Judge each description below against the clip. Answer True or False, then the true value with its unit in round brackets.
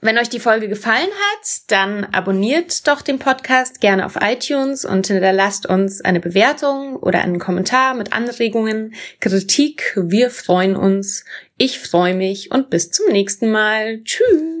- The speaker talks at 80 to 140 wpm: False (150 wpm)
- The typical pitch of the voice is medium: False (215 Hz)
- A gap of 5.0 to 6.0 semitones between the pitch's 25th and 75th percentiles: True (5.5 semitones)